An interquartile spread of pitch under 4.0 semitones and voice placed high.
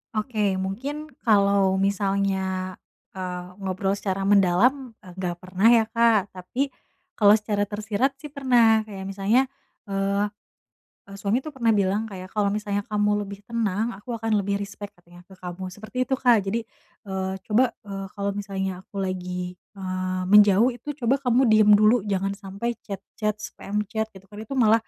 Yes: narrow, 2.6 semitones; high, 205 Hz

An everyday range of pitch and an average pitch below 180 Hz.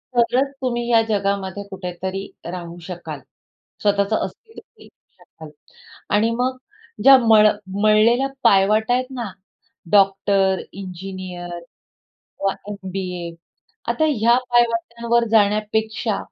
No: average, 3.6 semitones; high, 210 Hz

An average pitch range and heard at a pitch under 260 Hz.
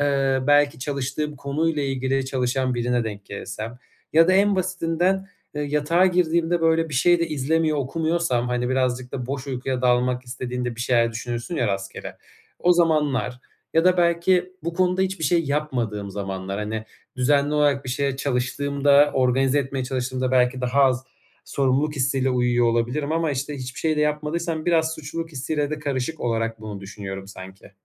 Yes: average, 4.3 semitones; low, 135 Hz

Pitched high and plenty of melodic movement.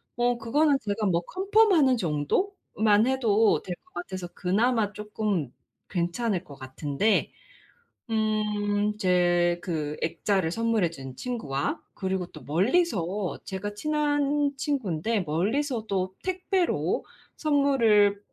Yes: high, 210 Hz; wide, 6.3 semitones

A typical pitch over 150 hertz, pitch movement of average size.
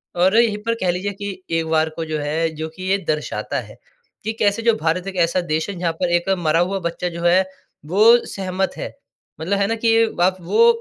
Yes: medium, 185 Hz; average, 3.5 semitones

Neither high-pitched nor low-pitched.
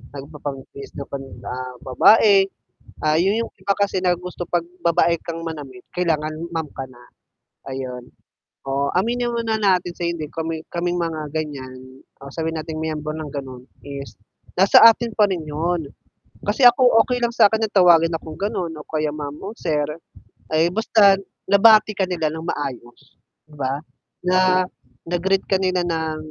Yes: medium, 165 Hz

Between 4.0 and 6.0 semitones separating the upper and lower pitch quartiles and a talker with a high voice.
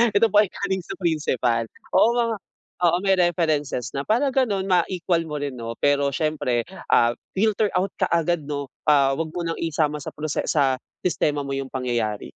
No: average, 5.0 semitones; medium, 155 Hz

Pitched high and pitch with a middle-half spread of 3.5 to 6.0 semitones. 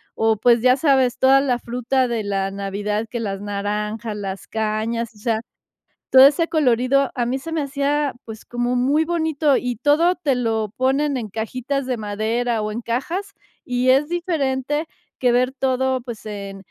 Yes: very high, 250 Hz; average, 3.9 semitones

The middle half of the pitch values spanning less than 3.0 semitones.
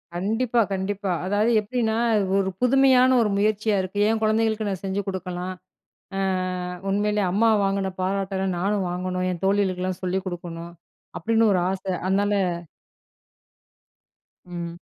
Yes: narrow, 2.6 semitones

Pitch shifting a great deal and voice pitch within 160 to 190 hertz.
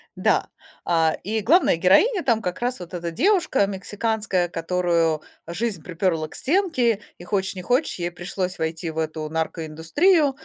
Yes: wide, 6.0 semitones; medium, 185 Hz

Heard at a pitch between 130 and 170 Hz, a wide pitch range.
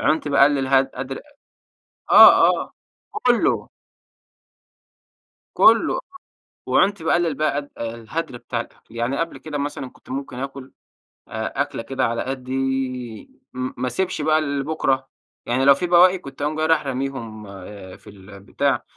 No: low, 135 Hz; average, 3.4 semitones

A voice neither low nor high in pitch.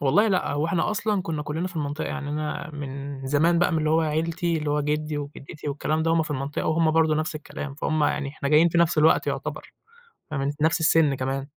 Yes: medium, 155 Hz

